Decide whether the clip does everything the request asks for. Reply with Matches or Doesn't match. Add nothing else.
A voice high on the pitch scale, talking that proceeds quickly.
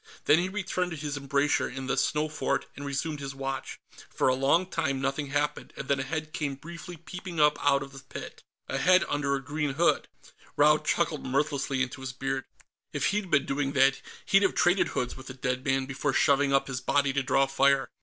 Doesn't match